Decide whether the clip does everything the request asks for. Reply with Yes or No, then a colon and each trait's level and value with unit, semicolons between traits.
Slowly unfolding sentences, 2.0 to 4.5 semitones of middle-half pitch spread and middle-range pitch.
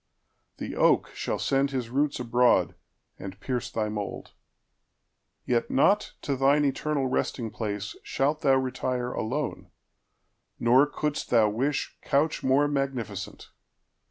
No: slow, 105 wpm; average, 3.2 semitones; low, 130 Hz